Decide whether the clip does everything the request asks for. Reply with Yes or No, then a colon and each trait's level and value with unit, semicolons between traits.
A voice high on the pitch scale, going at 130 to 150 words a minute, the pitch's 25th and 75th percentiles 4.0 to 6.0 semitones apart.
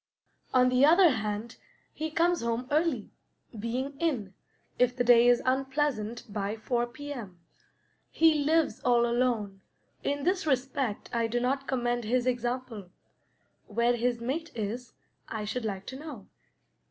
No: high, 245 Hz; average, 140 wpm; average, 3.4 semitones